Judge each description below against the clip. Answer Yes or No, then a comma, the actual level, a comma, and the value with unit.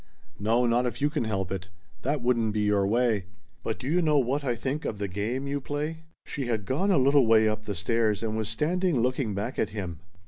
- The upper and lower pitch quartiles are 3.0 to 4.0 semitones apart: No, average, 4.7 semitones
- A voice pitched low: Yes, low, 120 Hz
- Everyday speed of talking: No, fast, 235 wpm